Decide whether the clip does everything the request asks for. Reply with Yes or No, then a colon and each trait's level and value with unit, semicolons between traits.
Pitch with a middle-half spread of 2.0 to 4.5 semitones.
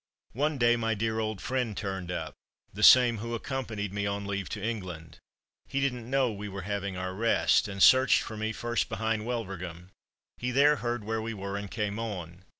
Yes: average, 3.1 semitones